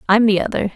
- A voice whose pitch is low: No, high, 205 Hz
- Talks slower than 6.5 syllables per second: No, 7.0 syllables/s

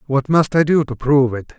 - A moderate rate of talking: No, fast, 265 wpm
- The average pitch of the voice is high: No, medium, 140 Hz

